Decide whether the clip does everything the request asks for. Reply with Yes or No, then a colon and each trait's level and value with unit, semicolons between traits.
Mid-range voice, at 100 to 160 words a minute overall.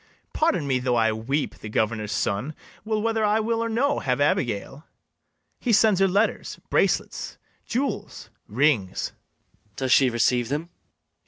Yes: medium, 145 Hz; average, 150 wpm